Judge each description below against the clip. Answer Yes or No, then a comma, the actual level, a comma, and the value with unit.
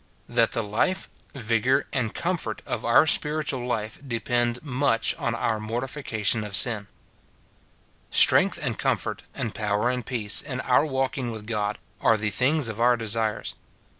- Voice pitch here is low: Yes, low, 115 Hz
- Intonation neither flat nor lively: Yes, average, 3.1 semitones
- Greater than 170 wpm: No, average, 155 wpm